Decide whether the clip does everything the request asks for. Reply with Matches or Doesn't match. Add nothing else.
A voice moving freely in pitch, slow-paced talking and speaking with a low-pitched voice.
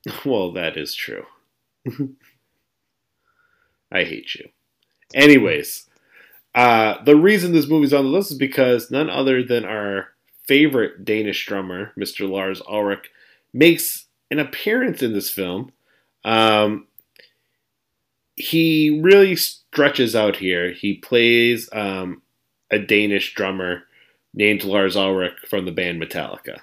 Matches